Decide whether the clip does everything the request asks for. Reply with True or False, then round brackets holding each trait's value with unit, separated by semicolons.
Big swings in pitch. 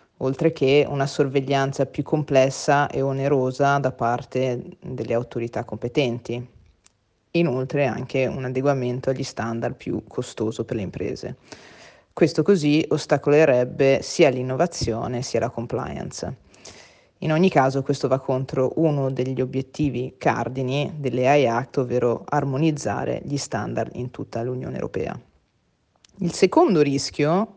False (2.8 semitones)